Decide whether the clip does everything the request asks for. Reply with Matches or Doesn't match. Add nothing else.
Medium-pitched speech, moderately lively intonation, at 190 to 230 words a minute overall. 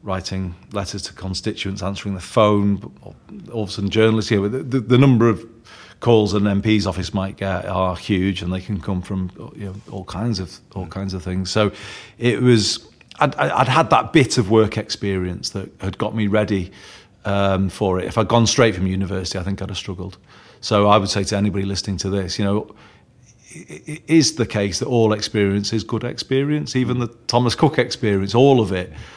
Doesn't match